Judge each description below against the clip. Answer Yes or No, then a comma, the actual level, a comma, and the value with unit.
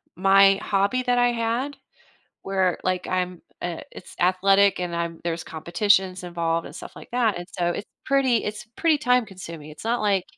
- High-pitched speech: Yes, high, 195 Hz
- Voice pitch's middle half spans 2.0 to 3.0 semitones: No, average, 4.4 semitones